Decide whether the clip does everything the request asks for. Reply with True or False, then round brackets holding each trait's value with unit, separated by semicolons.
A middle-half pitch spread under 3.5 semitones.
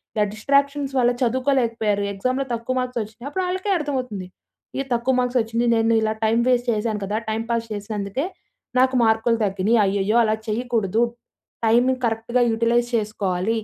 True (2.8 semitones)